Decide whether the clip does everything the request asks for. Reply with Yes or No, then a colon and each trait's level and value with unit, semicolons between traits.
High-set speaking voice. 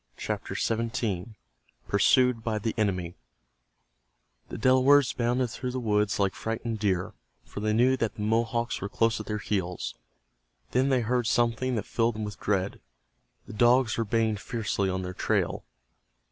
No: low, 115 Hz